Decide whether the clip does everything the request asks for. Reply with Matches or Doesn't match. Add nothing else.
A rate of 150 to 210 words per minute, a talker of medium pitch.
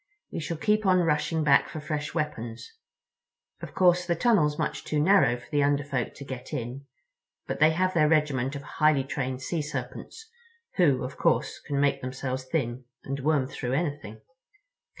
Matches